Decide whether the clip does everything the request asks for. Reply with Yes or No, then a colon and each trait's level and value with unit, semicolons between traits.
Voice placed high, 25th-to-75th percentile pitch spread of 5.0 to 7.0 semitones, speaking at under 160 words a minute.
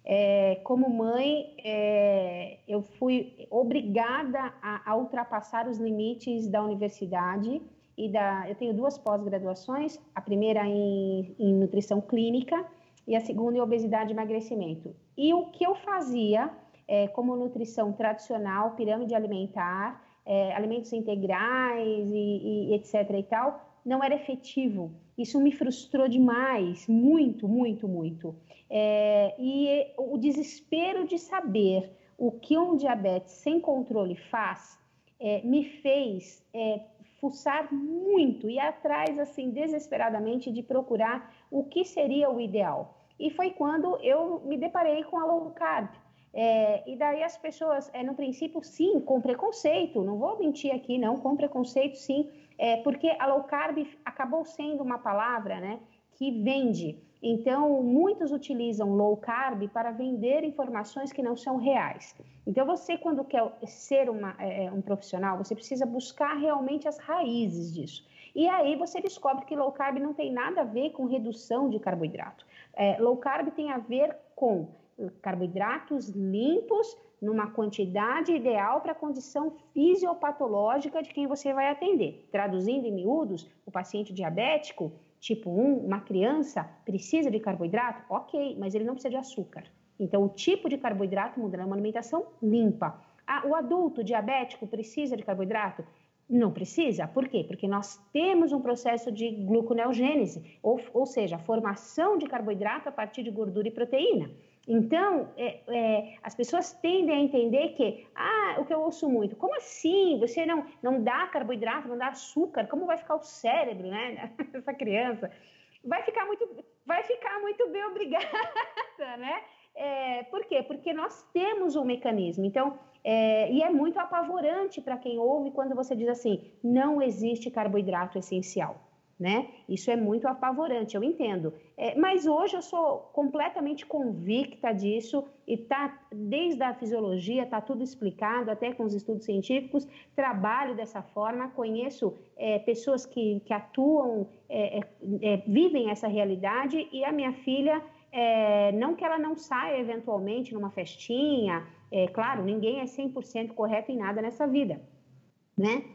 Yes: high, 245 Hz; wide, 5.6 semitones; average, 150 wpm